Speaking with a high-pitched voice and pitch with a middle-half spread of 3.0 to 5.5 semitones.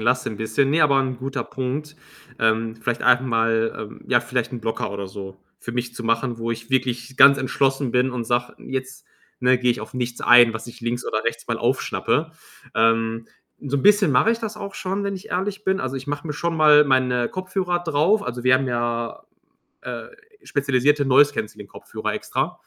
No: low, 125 Hz; average, 3.8 semitones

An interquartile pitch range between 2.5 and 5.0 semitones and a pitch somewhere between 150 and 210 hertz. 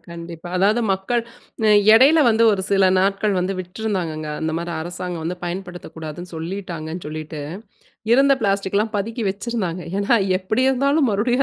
Yes: average, 4.3 semitones; high, 190 Hz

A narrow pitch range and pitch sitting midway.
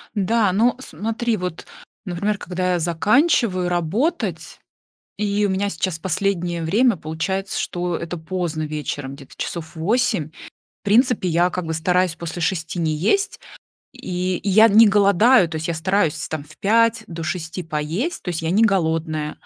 No: average, 4.2 semitones; medium, 180 Hz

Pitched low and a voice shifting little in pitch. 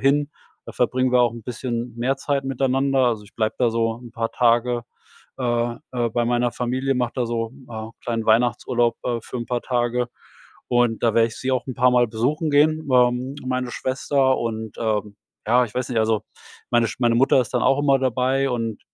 Yes: low, 120 Hz; narrow, 1.9 semitones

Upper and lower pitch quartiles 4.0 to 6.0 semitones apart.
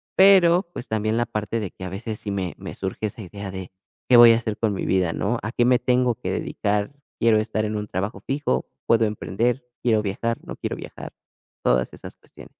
No: average, 3.0 semitones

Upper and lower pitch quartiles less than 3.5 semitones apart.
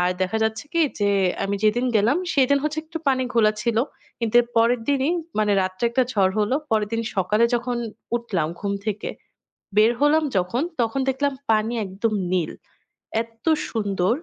No: average, 3.8 semitones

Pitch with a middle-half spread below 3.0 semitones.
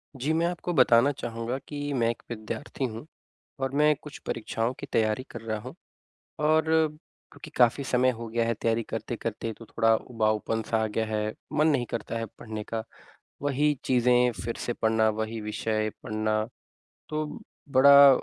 No: average, 3.7 semitones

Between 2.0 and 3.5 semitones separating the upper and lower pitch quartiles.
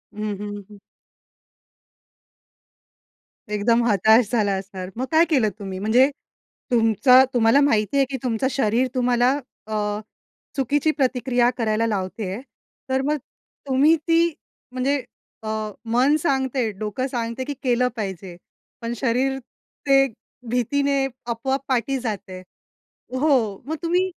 No: average, 4.0 semitones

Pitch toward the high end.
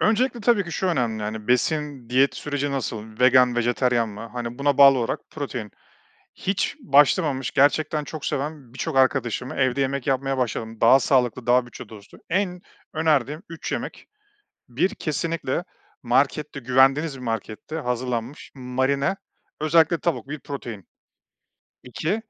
No: low, 135 Hz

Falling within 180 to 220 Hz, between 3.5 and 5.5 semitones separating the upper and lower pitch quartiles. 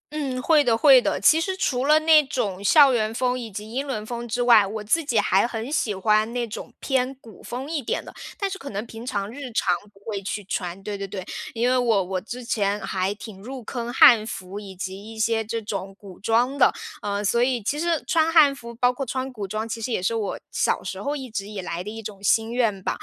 No: high, 230 Hz; average, 4.0 semitones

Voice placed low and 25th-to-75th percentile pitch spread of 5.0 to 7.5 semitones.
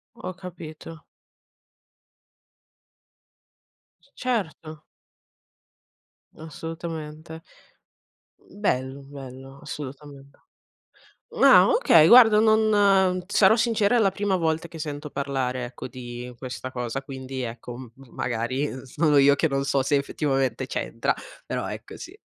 No: medium, 150 Hz; wide, 5.5 semitones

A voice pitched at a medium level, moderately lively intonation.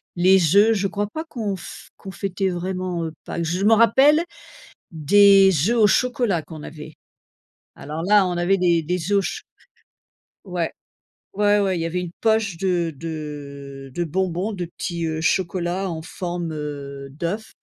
Yes: medium, 180 Hz; average, 3.5 semitones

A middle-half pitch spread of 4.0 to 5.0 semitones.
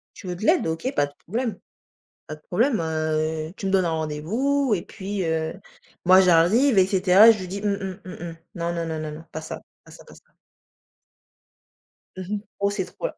Yes: average, 4.3 semitones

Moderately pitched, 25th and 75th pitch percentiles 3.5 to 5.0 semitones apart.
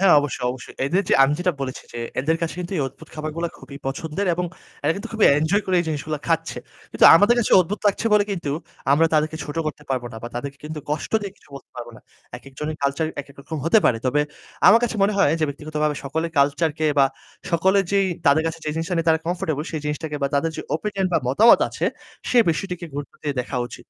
Yes: medium, 155 Hz; average, 3.9 semitones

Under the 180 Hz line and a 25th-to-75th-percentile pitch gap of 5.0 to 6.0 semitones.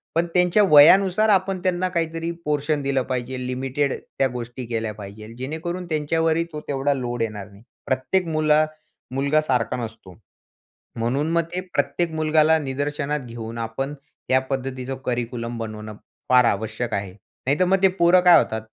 Yes: medium, 140 Hz; average, 5.3 semitones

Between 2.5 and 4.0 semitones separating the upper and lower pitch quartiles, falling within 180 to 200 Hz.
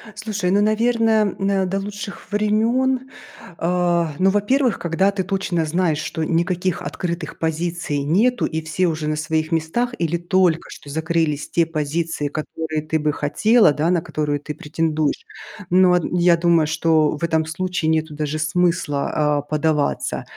No: average, 3.6 semitones; medium, 170 Hz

